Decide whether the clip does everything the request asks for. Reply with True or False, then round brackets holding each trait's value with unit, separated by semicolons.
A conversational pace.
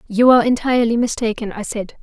True (180 wpm)